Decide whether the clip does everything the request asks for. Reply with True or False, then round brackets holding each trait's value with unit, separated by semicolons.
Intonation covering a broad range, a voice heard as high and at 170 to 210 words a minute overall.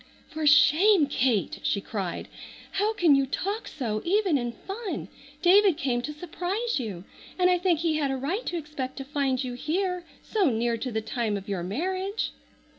True (7.0 semitones; 300 Hz; 185 wpm)